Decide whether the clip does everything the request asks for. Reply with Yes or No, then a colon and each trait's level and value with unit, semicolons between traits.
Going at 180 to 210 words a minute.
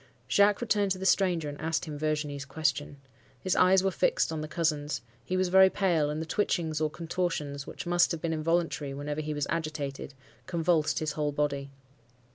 Yes: average, 190 wpm